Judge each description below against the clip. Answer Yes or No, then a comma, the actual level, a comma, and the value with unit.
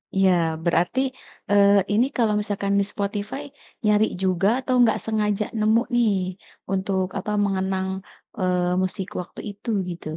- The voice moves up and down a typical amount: No, narrow, 2.1 semitones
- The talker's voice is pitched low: No, high, 200 Hz